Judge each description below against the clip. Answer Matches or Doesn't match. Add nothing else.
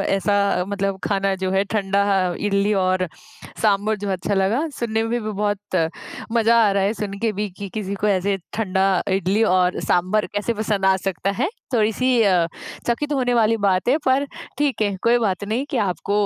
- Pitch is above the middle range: Matches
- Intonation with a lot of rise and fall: Doesn't match